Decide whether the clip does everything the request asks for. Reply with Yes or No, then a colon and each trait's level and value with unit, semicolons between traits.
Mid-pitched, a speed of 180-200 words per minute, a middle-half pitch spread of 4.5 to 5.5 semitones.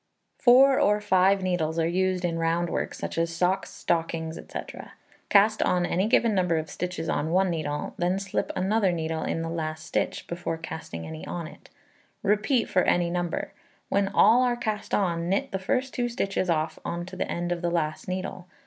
No: medium, 180 Hz; average, 195 wpm; average, 3.0 semitones